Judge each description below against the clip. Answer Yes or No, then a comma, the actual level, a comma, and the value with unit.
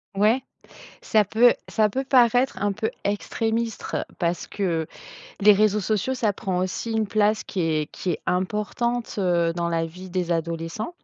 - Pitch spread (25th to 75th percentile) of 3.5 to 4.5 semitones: Yes, average, 3.9 semitones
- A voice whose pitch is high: Yes, high, 205 Hz